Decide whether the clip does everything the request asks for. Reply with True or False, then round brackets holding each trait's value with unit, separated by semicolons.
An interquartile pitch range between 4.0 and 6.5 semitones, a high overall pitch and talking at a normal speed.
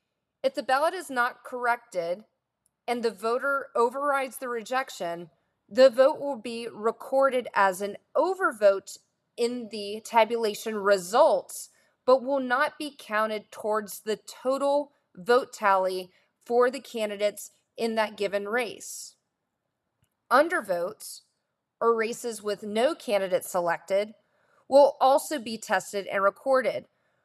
False (4.4 semitones; 235 Hz; 120 wpm)